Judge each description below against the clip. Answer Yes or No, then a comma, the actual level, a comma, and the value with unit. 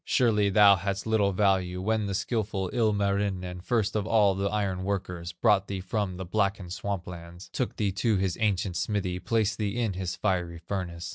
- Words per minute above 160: Yes, average, 185 wpm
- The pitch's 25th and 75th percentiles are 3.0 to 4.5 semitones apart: No, narrow, 2.4 semitones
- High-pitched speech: No, low, 100 Hz